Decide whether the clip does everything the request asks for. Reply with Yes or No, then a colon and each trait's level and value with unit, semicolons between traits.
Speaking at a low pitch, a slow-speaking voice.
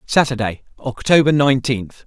Yes: low, 125 Hz; slow, 85 wpm